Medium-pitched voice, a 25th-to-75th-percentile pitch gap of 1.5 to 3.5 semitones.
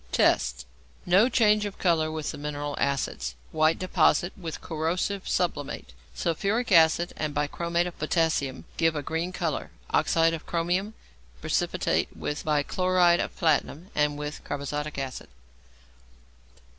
Yes: medium, 160 Hz; average, 3.2 semitones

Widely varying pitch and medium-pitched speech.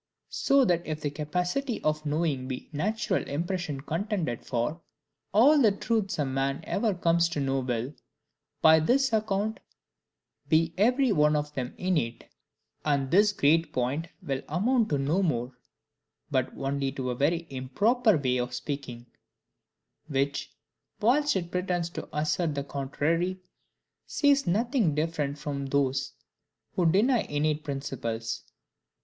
Yes: wide, 5.8 semitones; medium, 155 Hz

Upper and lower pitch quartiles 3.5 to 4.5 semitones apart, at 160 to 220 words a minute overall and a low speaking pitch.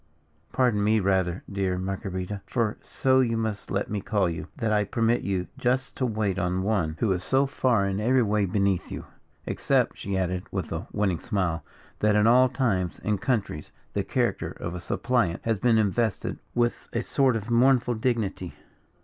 Yes: average, 4.0 semitones; average, 185 wpm; low, 105 Hz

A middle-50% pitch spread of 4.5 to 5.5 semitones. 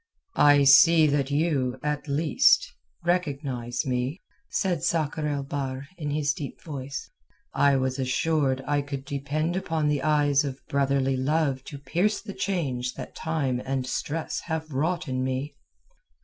No: average, 2.9 semitones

